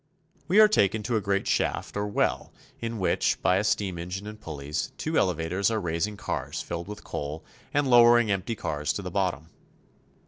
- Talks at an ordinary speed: Yes, average, 185 wpm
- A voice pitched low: Yes, low, 100 Hz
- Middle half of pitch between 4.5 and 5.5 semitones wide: Yes, average, 4.8 semitones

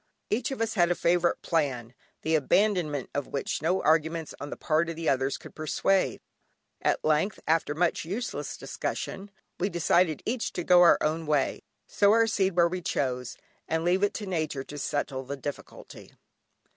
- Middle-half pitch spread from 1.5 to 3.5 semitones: No, average, 4.1 semitones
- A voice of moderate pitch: Yes, medium, 165 Hz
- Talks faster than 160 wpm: Yes, average, 180 wpm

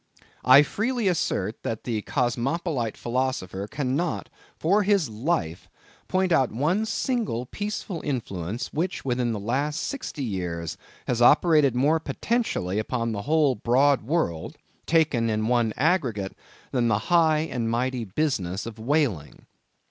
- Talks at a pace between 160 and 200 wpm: No, slow, 135 wpm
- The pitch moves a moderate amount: No, wide, 6.3 semitones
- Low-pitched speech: Yes, low, 130 Hz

